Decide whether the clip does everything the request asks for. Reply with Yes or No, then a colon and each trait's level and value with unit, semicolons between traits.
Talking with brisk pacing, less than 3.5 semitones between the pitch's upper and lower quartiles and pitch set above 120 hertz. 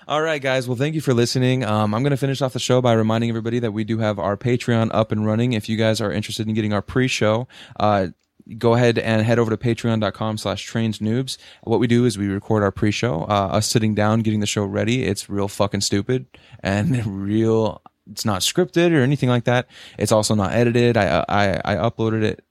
No: fast, 225 wpm; average, 2.7 semitones; low, 110 Hz